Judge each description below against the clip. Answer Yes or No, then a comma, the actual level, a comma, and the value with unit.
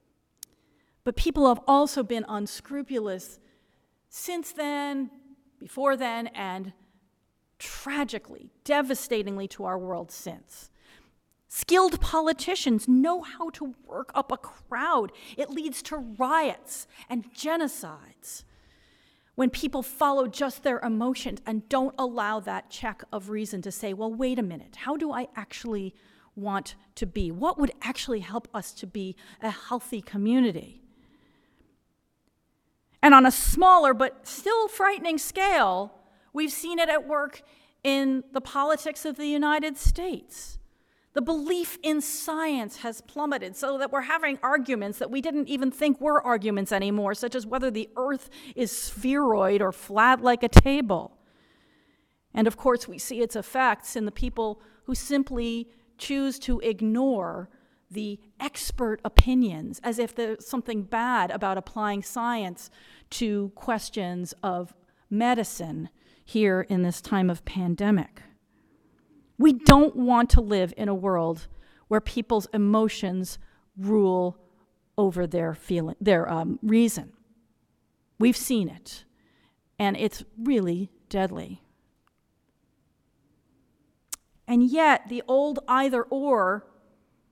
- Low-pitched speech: No, high, 240 Hz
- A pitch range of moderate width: Yes, average, 5.0 semitones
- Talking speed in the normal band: No, slow, 130 wpm